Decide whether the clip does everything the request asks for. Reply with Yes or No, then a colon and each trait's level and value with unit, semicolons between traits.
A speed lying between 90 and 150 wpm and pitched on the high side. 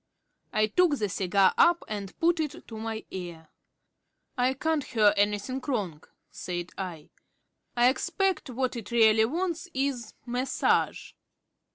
Yes: slow, 135 wpm; high, 235 Hz